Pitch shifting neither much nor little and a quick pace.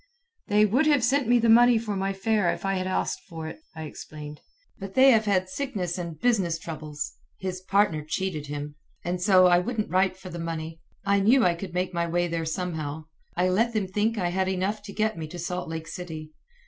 Yes: average, 4.0 semitones; fast, 220 wpm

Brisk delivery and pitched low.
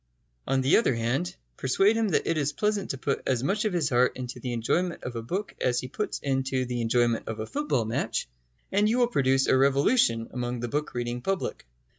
Yes: fast, 220 wpm; low, 130 Hz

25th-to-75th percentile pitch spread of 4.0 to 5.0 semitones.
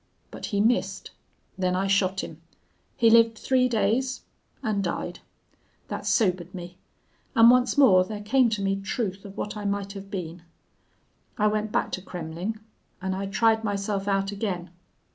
No: average, 2.8 semitones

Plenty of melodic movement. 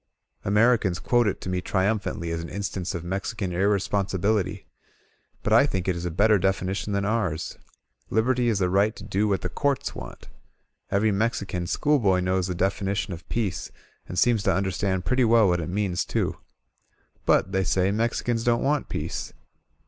No: average, 3.0 semitones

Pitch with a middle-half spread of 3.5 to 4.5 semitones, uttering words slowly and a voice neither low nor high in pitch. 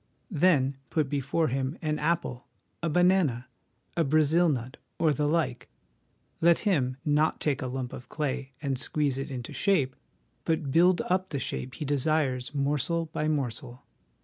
No: average, 3.8 semitones; average, 155 wpm; medium, 145 Hz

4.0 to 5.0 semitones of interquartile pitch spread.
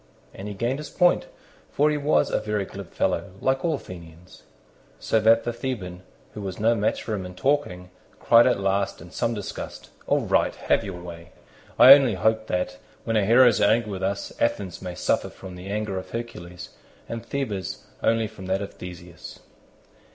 Yes: average, 4.3 semitones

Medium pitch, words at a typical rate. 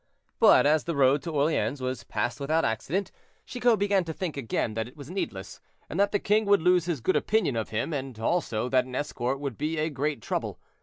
No: medium, 145 Hz; fast, 220 wpm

